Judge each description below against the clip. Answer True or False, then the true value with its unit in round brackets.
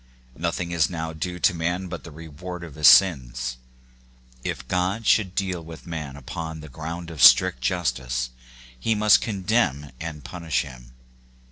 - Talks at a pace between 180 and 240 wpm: False (165 wpm)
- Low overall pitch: True (80 Hz)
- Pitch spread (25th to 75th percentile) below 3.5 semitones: False (4.2 semitones)